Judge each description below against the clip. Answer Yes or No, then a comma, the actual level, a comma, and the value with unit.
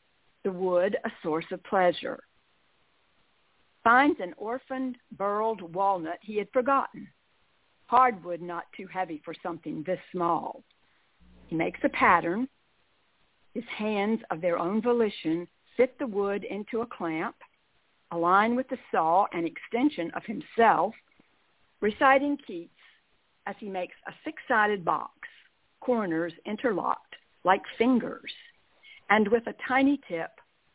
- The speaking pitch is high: Yes, high, 210 Hz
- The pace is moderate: No, slow, 125 wpm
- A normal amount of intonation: No, wide, 6.1 semitones